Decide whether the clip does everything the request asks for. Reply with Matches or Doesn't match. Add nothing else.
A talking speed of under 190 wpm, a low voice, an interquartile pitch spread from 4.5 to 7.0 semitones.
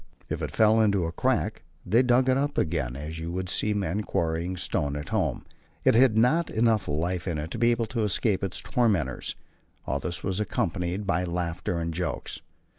Doesn't match